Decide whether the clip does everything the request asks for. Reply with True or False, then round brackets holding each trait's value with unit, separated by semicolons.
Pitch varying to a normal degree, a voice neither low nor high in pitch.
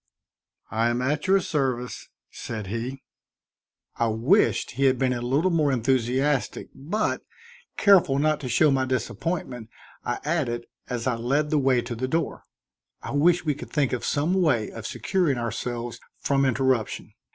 False (3.8 semitones; 130 Hz)